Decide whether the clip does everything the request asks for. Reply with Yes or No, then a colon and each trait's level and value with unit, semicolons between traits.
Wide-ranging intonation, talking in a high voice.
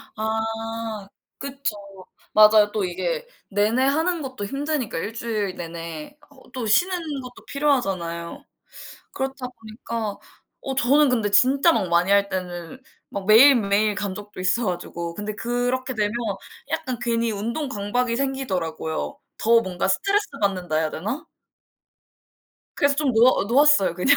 No: average, 4.9 semitones; high, 225 Hz